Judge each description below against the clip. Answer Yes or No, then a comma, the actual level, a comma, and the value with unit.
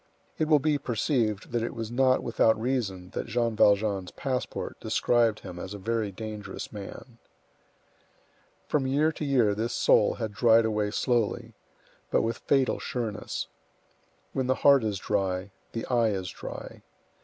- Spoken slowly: No, average, 155 wpm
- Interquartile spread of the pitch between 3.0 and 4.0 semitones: Yes, average, 3.6 semitones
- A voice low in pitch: Yes, low, 115 Hz